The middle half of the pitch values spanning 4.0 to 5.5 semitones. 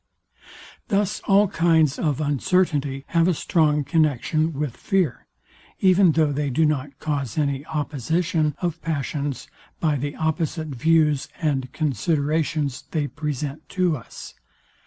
No: narrow, 2.5 semitones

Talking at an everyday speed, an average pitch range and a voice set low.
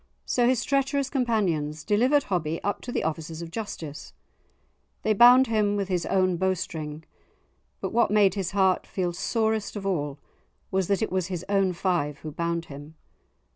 No: average, 170 wpm; average, 4.7 semitones; high, 190 Hz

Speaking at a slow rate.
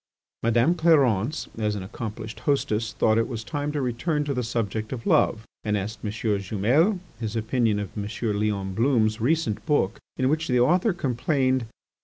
No: average, 170 wpm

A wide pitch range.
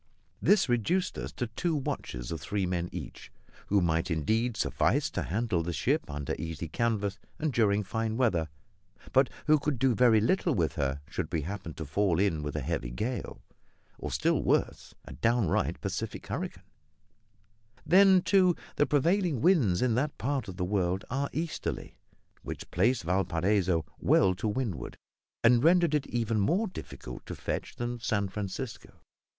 Yes: wide, 7.2 semitones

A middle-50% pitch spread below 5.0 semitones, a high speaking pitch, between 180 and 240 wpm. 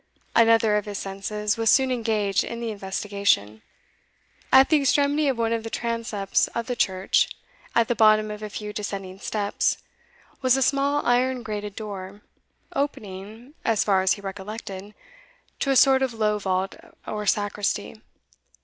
No: average, 2.9 semitones; high, 215 Hz; average, 160 wpm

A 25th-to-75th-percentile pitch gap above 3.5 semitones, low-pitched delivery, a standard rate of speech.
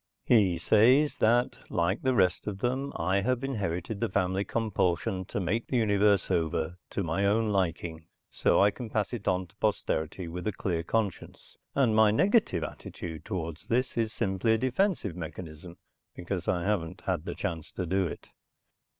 Yes: average, 4.4 semitones; very low, 95 Hz; average, 175 wpm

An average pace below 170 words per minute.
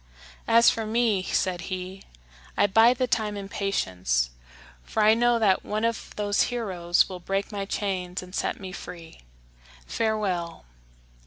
Yes: average, 150 wpm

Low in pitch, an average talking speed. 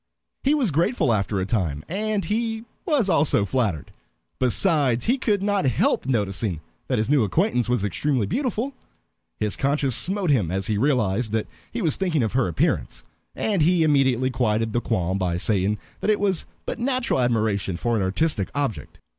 Yes: low, 130 Hz; average, 175 wpm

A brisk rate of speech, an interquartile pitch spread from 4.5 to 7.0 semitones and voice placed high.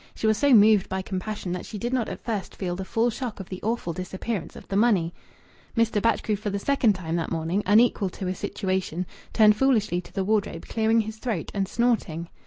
No: fast, 215 wpm; average, 3.4 semitones; high, 205 Hz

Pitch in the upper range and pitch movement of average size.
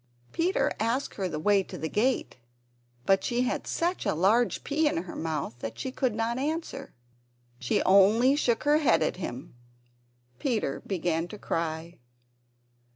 No: high, 210 Hz; wide, 7.6 semitones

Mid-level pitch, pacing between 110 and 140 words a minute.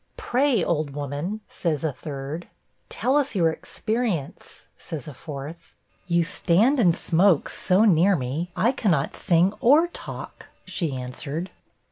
Yes: medium, 170 Hz; slow, 135 wpm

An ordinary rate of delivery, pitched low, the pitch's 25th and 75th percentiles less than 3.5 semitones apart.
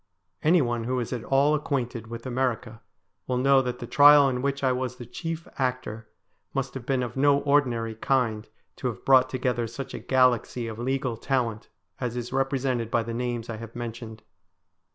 Yes: average, 185 wpm; low, 125 Hz; narrow, 2.5 semitones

